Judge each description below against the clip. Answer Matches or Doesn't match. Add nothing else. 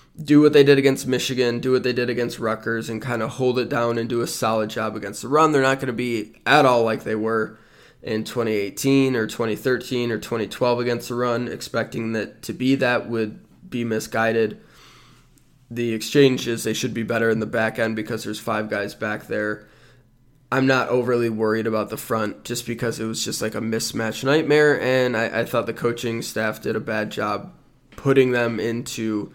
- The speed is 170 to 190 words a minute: Doesn't match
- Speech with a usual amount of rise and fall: Doesn't match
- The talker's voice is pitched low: Matches